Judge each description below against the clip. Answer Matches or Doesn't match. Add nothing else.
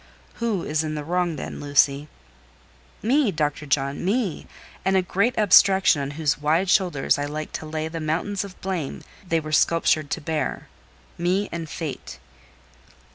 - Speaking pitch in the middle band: Matches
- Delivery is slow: Doesn't match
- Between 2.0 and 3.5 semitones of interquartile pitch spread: Doesn't match